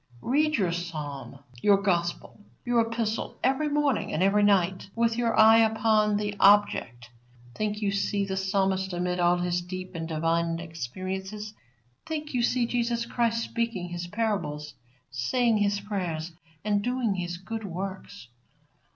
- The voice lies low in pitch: No, high, 200 Hz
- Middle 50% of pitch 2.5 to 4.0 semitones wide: No, average, 4.4 semitones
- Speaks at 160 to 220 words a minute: No, average, 145 wpm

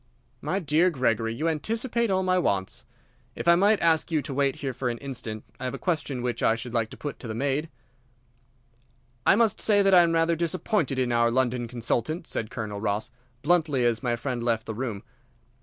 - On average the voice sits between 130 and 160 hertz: Yes, low, 135 Hz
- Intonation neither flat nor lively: No, wide, 6.3 semitones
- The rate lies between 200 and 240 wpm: Yes, fast, 205 wpm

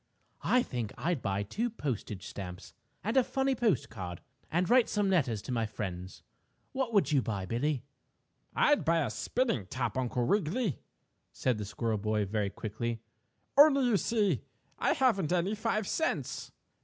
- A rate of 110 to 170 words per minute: Yes, average, 160 wpm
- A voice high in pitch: No, low, 135 Hz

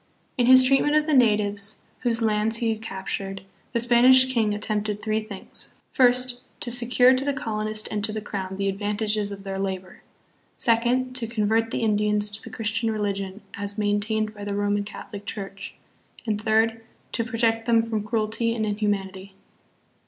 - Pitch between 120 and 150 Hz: No, high, 215 Hz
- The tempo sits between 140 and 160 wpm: No, average, 175 wpm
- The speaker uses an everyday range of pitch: No, narrow, 2.2 semitones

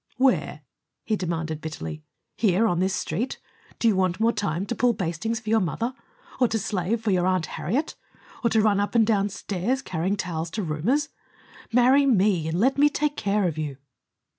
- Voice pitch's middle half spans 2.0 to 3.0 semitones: No, average, 5.0 semitones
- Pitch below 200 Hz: No, high, 205 Hz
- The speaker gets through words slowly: No, average, 190 wpm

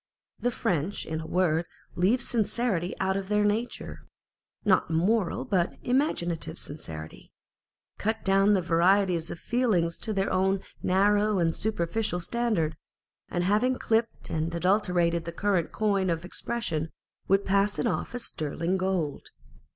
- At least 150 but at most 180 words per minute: No, average, 140 wpm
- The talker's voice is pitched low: No, high, 190 Hz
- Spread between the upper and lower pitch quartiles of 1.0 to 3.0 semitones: No, average, 3.9 semitones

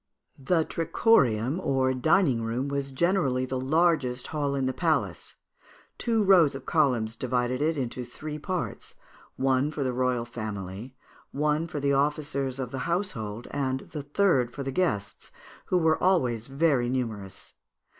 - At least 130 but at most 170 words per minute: Yes, average, 150 wpm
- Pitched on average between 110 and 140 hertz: Yes, low, 135 Hz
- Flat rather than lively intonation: No, average, 4.0 semitones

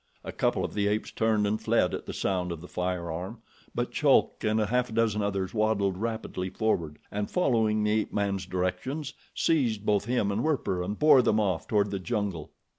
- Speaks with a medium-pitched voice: No, low, 105 Hz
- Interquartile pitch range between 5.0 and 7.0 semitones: No, average, 2.9 semitones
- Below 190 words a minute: No, average, 195 wpm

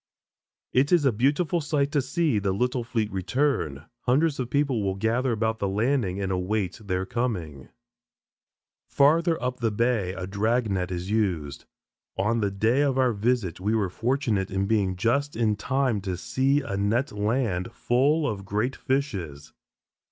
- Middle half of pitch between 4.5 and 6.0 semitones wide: Yes, wide, 5.4 semitones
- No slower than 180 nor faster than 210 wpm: No, average, 165 wpm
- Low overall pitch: Yes, low, 110 Hz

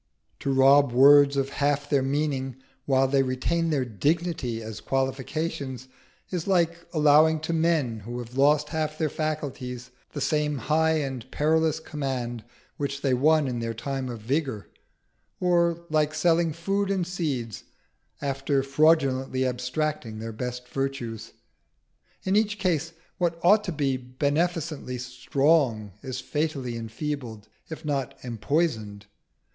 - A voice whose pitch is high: No, medium, 140 Hz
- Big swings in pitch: No, average, 4.0 semitones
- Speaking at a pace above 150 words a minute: No, slow, 135 wpm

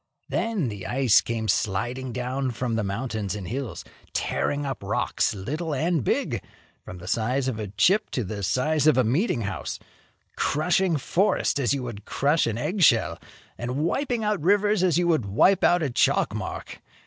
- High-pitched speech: No, low, 130 Hz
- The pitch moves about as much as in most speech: No, wide, 6.9 semitones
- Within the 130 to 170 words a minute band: No, average, 180 wpm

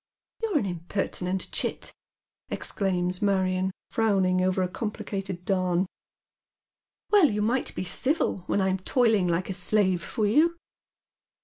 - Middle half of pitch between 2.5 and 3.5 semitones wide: Yes, average, 2.8 semitones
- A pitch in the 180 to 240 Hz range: Yes, high, 190 Hz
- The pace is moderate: No, slow, 130 wpm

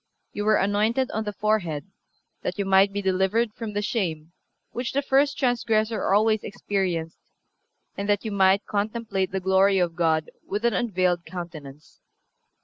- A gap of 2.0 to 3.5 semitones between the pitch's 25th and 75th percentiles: Yes, average, 2.9 semitones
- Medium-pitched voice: No, high, 200 Hz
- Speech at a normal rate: Yes, average, 155 wpm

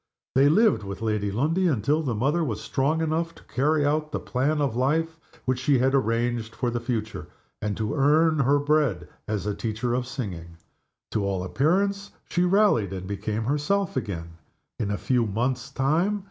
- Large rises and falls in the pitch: Yes, wide, 6.0 semitones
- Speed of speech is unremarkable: Yes, average, 180 wpm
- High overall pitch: No, low, 130 Hz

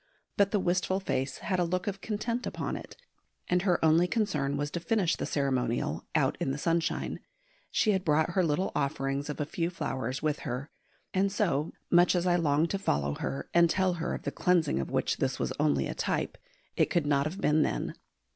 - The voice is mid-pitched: Yes, medium, 165 Hz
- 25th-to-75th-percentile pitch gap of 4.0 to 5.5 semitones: Yes, average, 4.7 semitones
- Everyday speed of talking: No, fast, 210 wpm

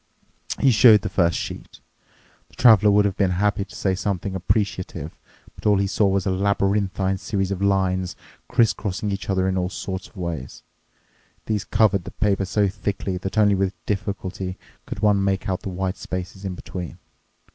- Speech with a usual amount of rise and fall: No, narrow, 1.6 semitones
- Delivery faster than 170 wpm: Yes, average, 180 wpm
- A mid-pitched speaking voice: No, very low, 95 Hz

